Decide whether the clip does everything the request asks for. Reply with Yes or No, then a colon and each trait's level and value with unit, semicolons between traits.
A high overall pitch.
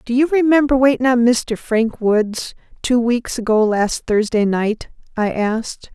Yes: high, 235 Hz